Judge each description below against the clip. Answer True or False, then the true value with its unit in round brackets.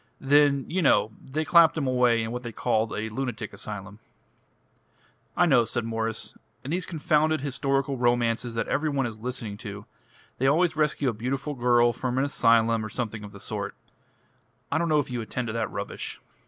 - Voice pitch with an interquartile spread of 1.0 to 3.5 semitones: False (3.9 semitones)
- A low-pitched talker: True (125 Hz)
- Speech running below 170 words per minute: False (190 wpm)